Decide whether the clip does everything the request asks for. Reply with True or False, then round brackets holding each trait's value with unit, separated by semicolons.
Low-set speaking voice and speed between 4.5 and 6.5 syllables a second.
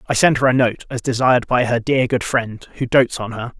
True (120 Hz; 5.5 syllables/s)